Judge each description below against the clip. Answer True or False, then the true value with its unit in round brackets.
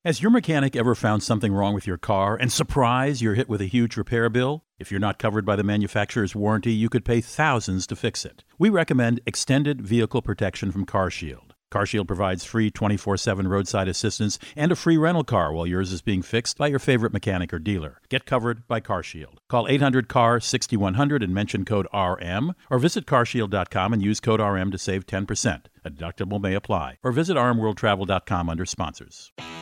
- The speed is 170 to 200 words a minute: True (190 wpm)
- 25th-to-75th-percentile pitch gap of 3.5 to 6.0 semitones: True (4.2 semitones)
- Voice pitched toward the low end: True (110 Hz)